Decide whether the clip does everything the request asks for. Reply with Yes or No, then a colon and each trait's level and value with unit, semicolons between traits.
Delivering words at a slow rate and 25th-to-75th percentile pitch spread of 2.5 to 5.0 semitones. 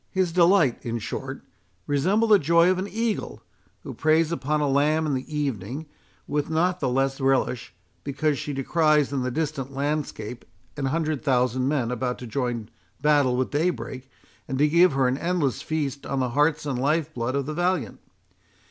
No: average, 175 wpm; average, 3.4 semitones